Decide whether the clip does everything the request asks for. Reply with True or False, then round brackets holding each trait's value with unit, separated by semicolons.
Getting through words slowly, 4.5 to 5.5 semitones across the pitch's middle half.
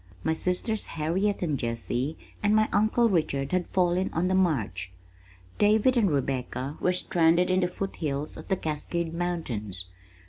False (160 wpm; 5.1 semitones)